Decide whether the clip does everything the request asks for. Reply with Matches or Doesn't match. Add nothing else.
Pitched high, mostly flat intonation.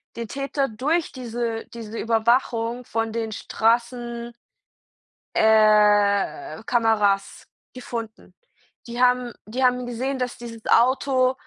Matches